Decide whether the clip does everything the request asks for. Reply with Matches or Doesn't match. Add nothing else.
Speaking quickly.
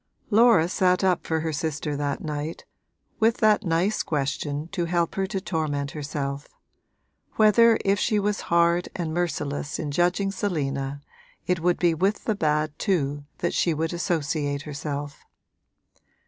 Doesn't match